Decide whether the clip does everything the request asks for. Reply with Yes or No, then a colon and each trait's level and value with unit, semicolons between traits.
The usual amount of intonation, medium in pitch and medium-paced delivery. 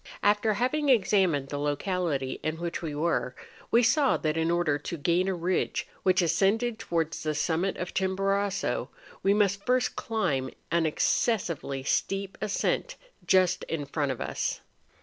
Yes: average, 4.4 semitones; medium, 180 Hz; average, 150 wpm